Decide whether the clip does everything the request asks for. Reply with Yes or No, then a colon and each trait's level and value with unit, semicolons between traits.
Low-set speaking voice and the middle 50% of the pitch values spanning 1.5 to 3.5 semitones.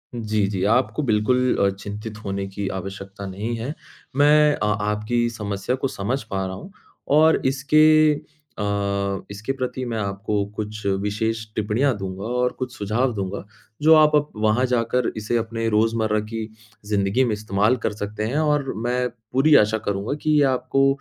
No: low, 110 Hz; average, 4.1 semitones